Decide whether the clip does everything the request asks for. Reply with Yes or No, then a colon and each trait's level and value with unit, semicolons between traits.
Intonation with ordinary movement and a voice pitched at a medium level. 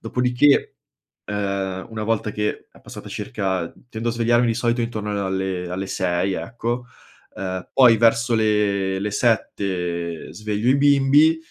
No: average, 3.7 semitones; low, 105 Hz